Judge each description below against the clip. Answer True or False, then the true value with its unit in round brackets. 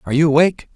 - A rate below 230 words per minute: False (235 wpm)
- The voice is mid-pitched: True (150 Hz)